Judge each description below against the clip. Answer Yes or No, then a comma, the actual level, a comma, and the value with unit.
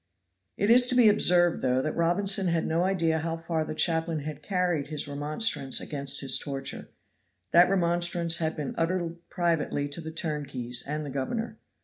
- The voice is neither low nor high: Yes, medium, 165 Hz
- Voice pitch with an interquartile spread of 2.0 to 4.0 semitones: Yes, average, 3.2 semitones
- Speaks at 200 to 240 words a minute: No, average, 170 wpm